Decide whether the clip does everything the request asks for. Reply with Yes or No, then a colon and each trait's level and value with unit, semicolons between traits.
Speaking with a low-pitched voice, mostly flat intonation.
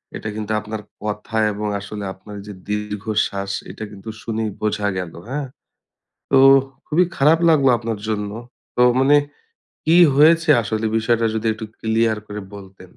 Yes: low, 110 Hz; narrow, 2.3 semitones